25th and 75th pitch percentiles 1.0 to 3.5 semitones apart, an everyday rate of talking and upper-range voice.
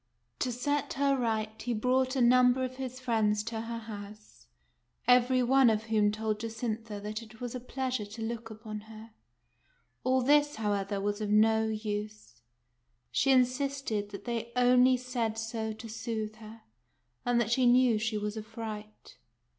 Yes: narrow, 2.6 semitones; average, 170 wpm; high, 225 Hz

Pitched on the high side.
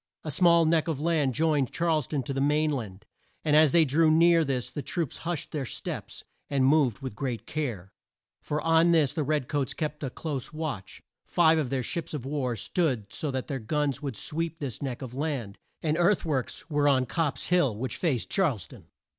No: medium, 145 Hz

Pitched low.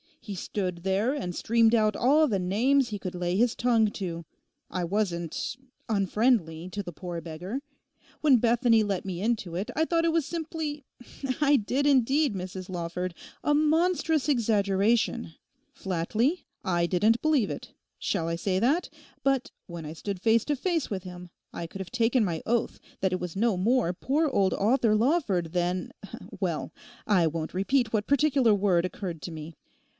No: high, 210 Hz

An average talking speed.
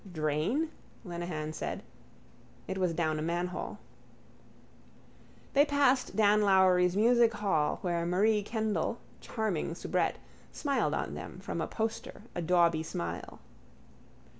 No: slow, 115 wpm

